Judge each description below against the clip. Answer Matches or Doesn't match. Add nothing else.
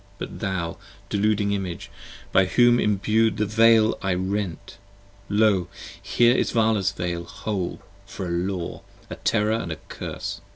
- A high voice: Doesn't match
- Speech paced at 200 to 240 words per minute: Doesn't match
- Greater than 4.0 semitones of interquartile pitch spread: Doesn't match